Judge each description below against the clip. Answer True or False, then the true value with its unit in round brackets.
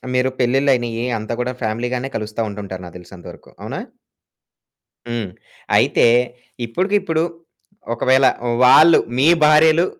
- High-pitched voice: False (125 Hz)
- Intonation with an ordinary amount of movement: False (5.7 semitones)